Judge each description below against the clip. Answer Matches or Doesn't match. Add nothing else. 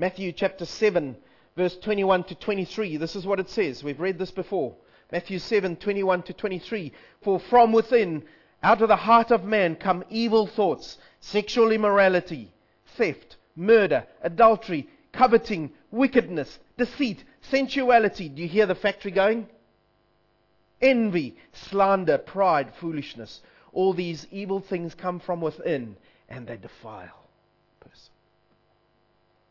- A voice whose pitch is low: Doesn't match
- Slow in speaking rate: Matches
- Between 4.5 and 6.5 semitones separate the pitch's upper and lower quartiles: Doesn't match